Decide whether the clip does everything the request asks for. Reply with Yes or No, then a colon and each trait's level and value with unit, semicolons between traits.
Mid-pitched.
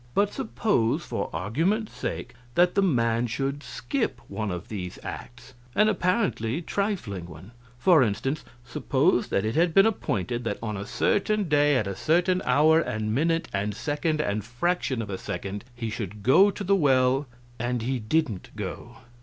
No: low, 130 Hz